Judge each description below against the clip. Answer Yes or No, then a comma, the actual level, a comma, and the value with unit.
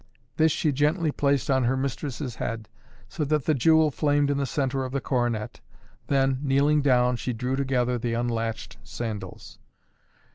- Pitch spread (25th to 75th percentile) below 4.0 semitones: Yes, average, 2.9 semitones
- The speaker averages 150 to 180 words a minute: Yes, average, 160 wpm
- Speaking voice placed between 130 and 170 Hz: Yes, low, 135 Hz